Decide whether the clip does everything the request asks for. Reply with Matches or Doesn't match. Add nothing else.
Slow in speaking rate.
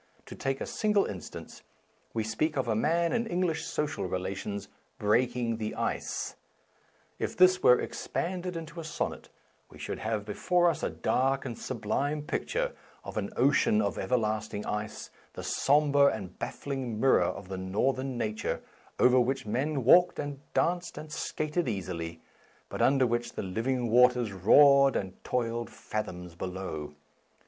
Doesn't match